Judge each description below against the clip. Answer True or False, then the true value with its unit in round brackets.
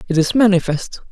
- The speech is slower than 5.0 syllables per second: False (5.6 syllables/s)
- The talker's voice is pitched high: True (200 Hz)